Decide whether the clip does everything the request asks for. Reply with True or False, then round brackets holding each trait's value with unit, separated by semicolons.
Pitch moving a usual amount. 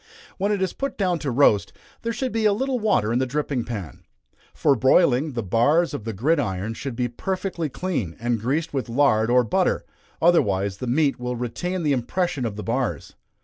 False (7.0 semitones)